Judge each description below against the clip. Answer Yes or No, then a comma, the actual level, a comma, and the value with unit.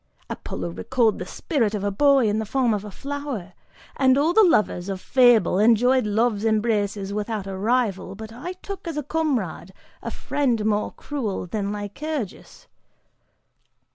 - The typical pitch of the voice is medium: No, high, 220 Hz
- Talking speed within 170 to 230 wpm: No, average, 160 wpm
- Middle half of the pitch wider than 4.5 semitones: Yes, average, 4.9 semitones